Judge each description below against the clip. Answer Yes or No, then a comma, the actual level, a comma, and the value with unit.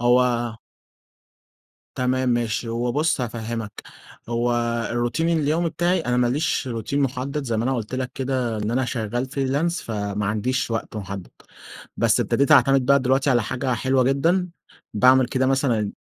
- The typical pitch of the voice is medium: No, low, 125 Hz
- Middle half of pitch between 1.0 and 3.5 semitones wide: Yes, average, 2.8 semitones